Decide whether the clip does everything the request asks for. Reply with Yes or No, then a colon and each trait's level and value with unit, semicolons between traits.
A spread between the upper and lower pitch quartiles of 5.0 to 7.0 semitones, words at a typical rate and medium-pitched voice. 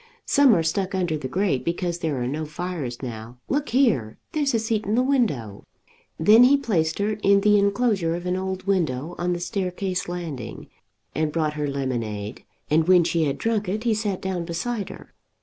Yes: wide, 5.4 semitones; average, 195 wpm; medium, 180 Hz